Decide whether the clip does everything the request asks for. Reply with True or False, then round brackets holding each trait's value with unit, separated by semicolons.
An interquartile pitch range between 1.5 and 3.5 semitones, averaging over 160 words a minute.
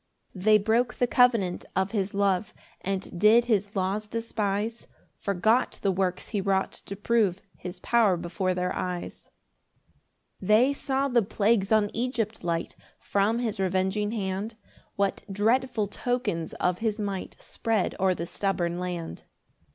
False (3.2 semitones; 145 wpm)